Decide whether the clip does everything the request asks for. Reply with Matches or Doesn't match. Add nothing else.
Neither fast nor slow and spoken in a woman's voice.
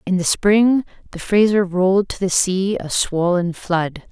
Matches